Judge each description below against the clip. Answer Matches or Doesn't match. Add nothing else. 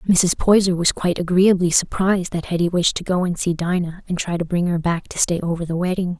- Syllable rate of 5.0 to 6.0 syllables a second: Matches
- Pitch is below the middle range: Doesn't match